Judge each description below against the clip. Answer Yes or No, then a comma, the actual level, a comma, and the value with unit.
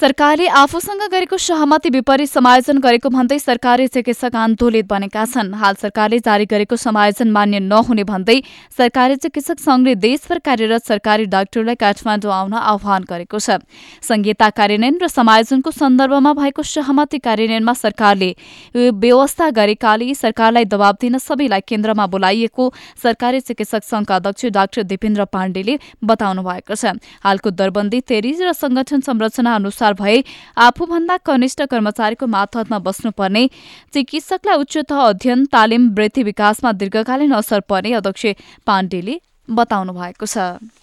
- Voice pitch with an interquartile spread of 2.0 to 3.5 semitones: No, average, 4.3 semitones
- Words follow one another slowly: Yes, slow, 130 wpm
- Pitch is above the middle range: Yes, high, 230 Hz